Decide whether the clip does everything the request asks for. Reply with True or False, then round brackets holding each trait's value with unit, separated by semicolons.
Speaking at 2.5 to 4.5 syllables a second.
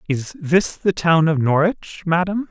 True (3.9 syllables/s)